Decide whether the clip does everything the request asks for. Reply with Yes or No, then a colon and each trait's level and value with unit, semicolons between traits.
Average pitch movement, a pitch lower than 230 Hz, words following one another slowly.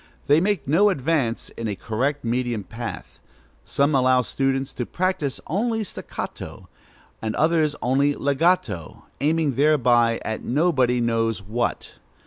Yes: average, 4.8 semitones; low, 135 Hz; slow, 125 wpm